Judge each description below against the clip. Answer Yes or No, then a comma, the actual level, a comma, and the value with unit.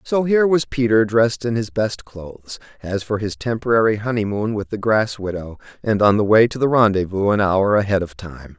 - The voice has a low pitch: Yes, low, 110 Hz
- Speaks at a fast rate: Yes, fast, 210 wpm